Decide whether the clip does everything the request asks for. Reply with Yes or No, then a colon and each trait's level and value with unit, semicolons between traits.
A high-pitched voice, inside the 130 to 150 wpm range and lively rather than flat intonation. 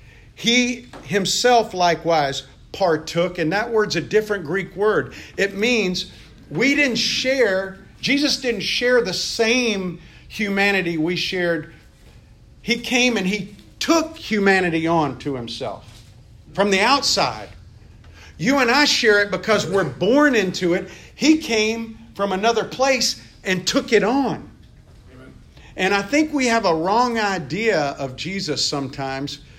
Yes: high, 195 Hz; slow, 135 wpm; wide, 6.3 semitones